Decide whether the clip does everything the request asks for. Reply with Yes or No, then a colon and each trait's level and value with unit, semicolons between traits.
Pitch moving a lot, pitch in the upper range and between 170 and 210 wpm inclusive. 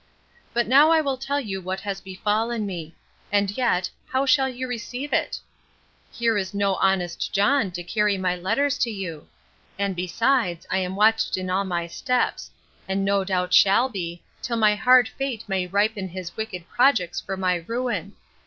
No: average, 4.5 semitones; high, 200 Hz; average, 175 wpm